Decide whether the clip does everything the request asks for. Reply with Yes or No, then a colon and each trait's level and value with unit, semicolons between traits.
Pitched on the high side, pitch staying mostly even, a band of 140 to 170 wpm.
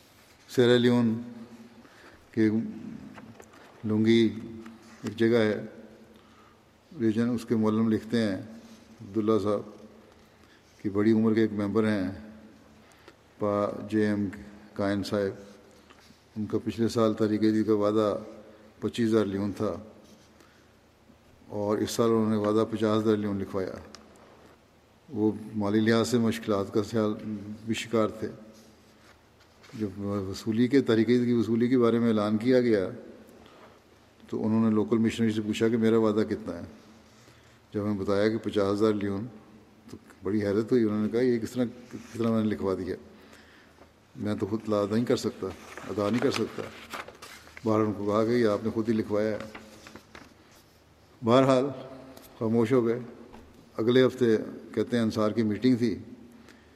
No: low, 110 Hz; narrow, 1.4 semitones; average, 145 wpm